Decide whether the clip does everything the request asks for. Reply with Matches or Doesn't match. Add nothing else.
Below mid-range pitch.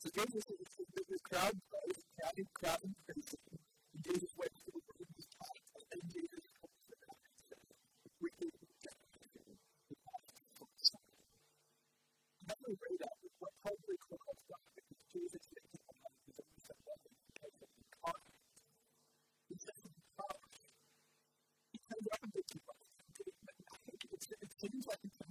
Doesn't match